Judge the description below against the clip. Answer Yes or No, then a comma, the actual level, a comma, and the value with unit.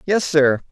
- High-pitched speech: No, medium, 160 Hz